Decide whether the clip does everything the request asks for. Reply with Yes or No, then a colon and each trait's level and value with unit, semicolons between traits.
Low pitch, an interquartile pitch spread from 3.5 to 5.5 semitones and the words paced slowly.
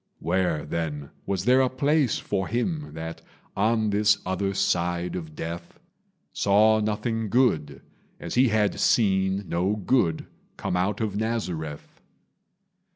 Yes: low, 100 Hz; average, 4.4 semitones; slow, 130 wpm